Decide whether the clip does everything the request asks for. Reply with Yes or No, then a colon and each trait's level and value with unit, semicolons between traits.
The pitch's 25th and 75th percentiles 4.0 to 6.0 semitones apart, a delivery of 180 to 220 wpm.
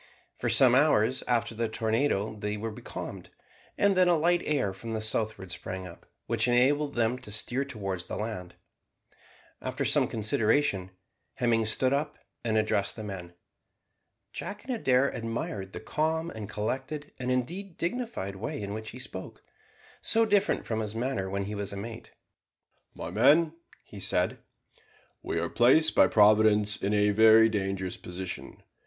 No: average, 5.0 semitones; average, 160 wpm